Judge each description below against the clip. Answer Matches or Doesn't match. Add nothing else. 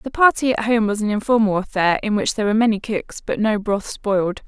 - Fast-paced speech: Matches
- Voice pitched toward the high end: Matches